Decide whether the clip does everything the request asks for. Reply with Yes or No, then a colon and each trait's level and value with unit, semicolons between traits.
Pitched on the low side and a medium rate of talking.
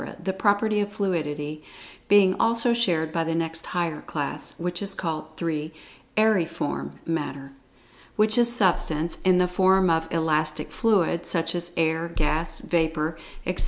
No: medium, 170 Hz; average, 145 wpm